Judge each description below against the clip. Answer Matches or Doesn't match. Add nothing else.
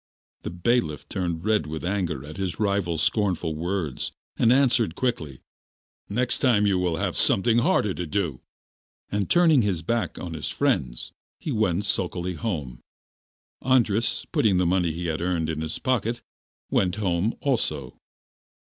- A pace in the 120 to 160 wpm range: Matches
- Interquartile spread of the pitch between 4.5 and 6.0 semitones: Matches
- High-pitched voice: Doesn't match